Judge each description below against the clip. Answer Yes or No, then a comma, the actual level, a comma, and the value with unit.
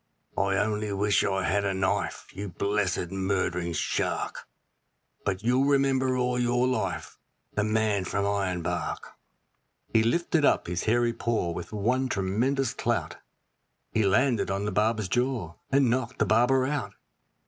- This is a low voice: Yes, low, 105 Hz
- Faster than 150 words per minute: No, average, 145 wpm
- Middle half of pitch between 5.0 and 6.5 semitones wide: No, average, 4.4 semitones